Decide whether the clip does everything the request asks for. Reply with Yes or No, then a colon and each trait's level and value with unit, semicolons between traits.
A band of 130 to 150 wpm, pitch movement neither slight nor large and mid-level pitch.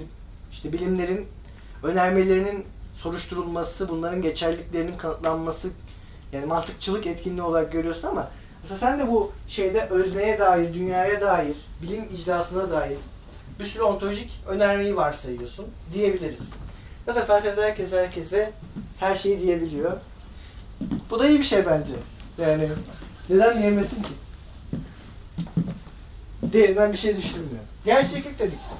No: average, 115 wpm; average, 3.7 semitones; medium, 180 Hz